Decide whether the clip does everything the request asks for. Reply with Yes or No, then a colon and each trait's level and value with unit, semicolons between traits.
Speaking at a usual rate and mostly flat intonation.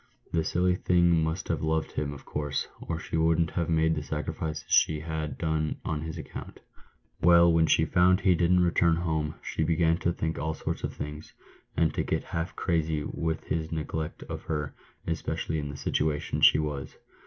Yes: average, 190 wpm; narrow, 1.4 semitones